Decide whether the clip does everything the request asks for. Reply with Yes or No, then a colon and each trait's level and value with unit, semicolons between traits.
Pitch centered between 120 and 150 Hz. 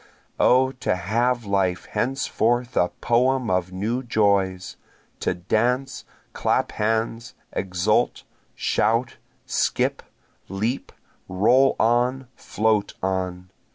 No: low, 110 Hz